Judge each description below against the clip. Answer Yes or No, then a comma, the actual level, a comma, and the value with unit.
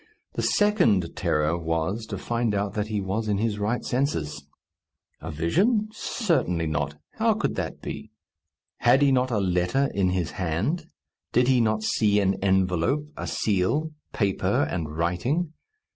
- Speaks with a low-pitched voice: Yes, low, 105 Hz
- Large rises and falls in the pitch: Yes, wide, 6.6 semitones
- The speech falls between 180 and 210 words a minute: No, average, 155 wpm